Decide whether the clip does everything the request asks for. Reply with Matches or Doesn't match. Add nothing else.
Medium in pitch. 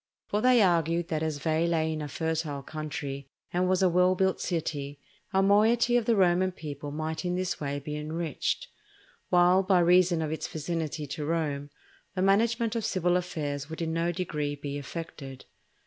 Matches